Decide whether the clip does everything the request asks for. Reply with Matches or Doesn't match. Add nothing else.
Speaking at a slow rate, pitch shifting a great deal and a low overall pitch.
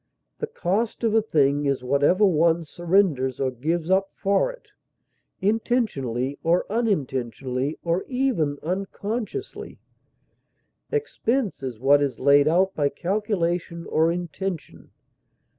Doesn't match